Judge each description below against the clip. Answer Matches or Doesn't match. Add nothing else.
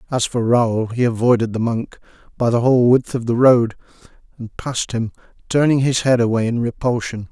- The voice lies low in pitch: Matches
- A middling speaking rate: Matches